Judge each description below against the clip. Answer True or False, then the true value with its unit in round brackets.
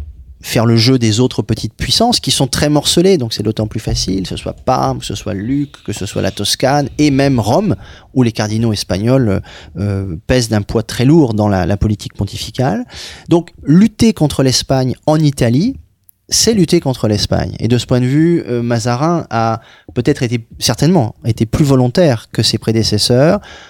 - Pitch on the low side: True (120 Hz)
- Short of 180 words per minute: False (190 wpm)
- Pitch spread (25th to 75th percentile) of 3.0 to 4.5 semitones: False (5.0 semitones)